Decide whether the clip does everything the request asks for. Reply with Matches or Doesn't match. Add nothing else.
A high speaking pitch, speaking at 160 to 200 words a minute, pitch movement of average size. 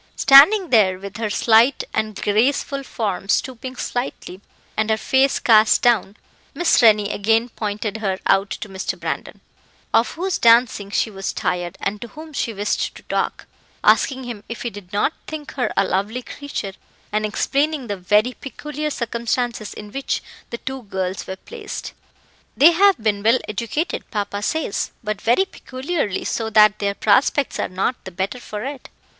Matches